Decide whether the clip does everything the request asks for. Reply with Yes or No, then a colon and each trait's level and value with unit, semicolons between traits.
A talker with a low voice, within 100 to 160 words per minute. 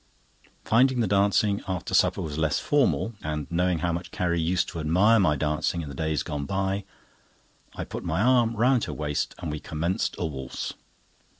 No: very low, 85 Hz; average, 185 wpm